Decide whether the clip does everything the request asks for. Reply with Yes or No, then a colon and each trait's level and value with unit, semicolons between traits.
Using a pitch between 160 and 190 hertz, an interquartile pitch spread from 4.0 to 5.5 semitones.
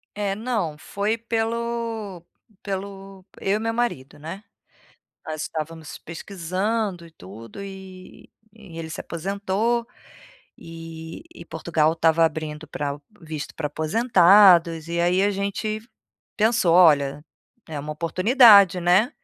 Yes: medium, 185 Hz; average, 4.6 semitones